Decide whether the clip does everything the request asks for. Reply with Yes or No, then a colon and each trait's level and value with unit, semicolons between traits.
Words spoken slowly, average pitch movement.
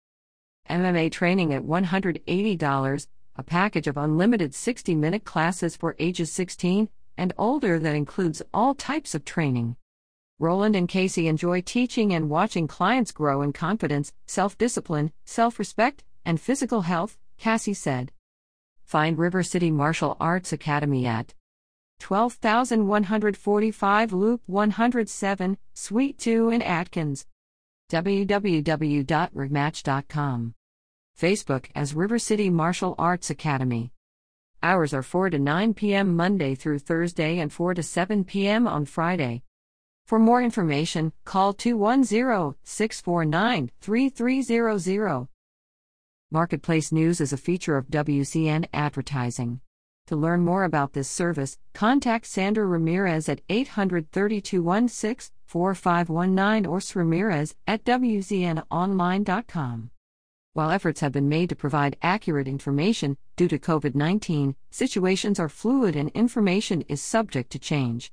No: slow, 115 wpm; wide, 5.9 semitones